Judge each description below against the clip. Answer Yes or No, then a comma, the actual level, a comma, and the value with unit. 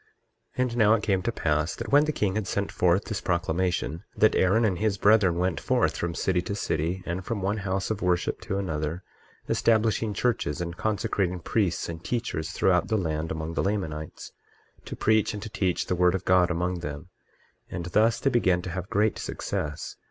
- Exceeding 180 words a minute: Yes, average, 200 wpm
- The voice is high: No, very low, 95 Hz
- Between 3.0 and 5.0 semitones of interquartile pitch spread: Yes, average, 3.6 semitones